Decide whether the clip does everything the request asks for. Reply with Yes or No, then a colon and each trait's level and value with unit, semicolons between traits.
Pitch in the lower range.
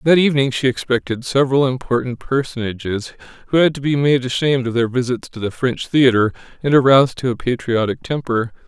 Yes: low, 130 Hz